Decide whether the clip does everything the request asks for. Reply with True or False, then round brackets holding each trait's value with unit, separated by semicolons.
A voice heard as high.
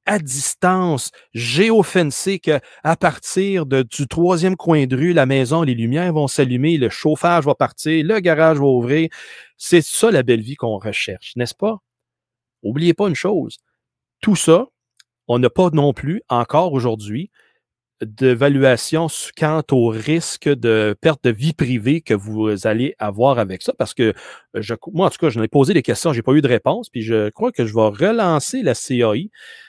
False (145 Hz)